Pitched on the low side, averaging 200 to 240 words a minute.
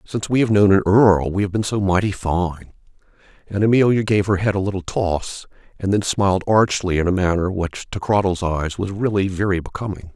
Yes: very low, 95 Hz; fast, 205 wpm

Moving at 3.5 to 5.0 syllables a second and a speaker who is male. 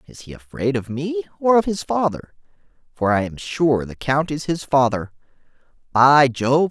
Yes: 4.5 syllables/s; male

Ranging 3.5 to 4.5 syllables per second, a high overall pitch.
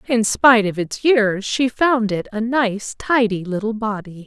Yes: 4.2 syllables/s; high, 220 Hz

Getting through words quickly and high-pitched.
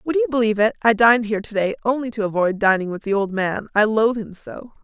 Yes: fast, 260 wpm; high, 220 Hz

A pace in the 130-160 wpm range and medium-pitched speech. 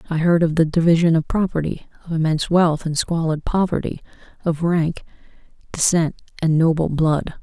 Yes: average, 155 wpm; medium, 165 Hz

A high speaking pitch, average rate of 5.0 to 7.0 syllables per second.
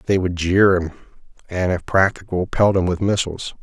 No: very low, 95 Hz; 5.7 syllables/s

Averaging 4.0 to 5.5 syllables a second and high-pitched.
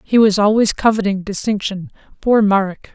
Yes: 5.1 syllables/s; high, 205 Hz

